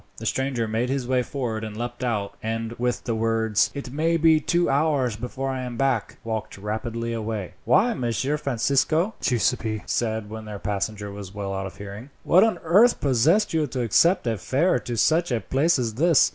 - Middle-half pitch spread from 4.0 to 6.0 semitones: Yes, average, 4.3 semitones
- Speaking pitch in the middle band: No, low, 120 Hz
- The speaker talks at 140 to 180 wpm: No, average, 195 wpm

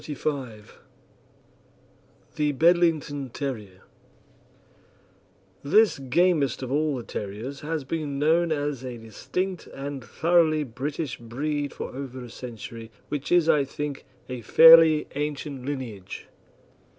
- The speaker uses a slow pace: Yes, slow, 115 wpm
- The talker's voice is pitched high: No, medium, 140 Hz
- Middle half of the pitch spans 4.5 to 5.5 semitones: No, average, 3.5 semitones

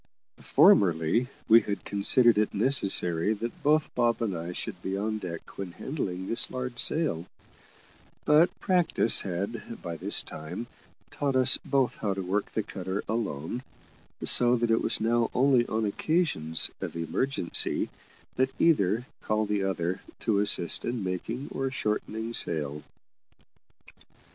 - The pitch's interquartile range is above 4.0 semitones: Yes, average, 5.1 semitones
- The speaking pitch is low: Yes, low, 110 Hz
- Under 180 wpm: Yes, average, 140 wpm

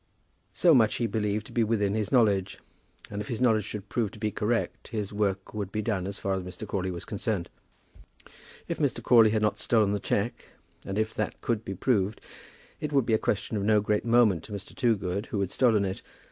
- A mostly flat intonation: Yes, narrow, 2.2 semitones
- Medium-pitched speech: No, low, 105 Hz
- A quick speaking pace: Yes, fast, 220 wpm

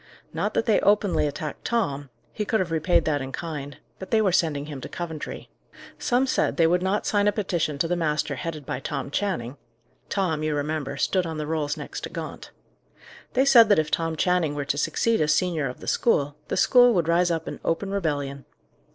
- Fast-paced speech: Yes, fast, 210 wpm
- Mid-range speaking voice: Yes, medium, 165 Hz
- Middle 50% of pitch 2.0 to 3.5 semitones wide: No, average, 4.7 semitones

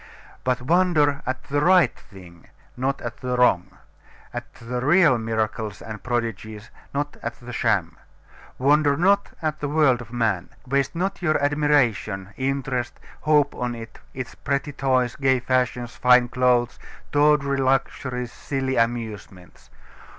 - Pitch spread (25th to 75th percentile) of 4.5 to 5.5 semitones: No, average, 3.7 semitones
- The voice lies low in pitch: Yes, low, 130 Hz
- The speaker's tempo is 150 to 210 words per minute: No, slow, 135 wpm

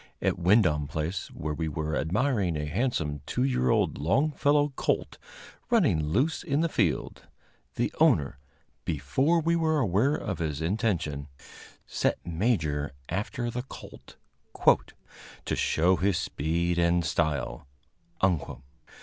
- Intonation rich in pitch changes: Yes, wide, 8.7 semitones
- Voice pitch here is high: No, very low, 90 Hz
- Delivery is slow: Yes, slow, 125 wpm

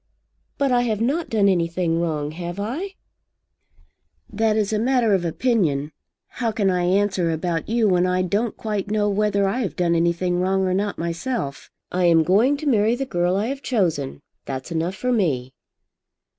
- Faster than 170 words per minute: Yes, average, 180 wpm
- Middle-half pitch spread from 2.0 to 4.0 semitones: No, average, 4.6 semitones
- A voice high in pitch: Yes, high, 195 Hz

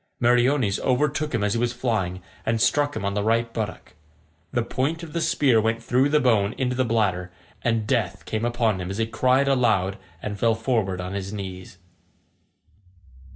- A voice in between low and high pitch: No, low, 115 Hz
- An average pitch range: Yes, average, 4.0 semitones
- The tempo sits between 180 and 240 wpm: Yes, average, 185 wpm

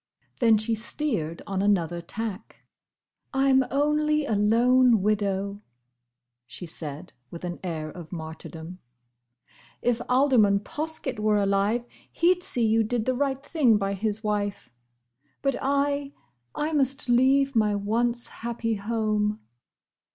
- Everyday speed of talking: No, slow, 130 wpm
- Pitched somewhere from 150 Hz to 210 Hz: No, high, 220 Hz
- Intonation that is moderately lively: Yes, average, 4.9 semitones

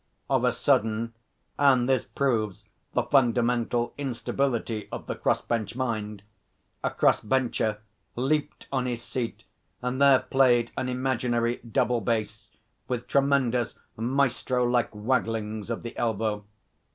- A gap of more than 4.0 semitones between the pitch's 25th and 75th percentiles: No, narrow, 2.5 semitones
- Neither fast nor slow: No, slow, 125 wpm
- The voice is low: Yes, low, 120 Hz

